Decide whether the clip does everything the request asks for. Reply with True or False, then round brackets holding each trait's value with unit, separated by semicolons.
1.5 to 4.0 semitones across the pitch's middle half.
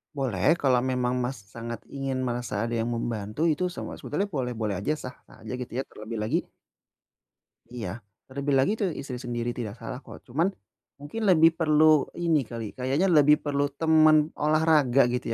False (4.4 semitones)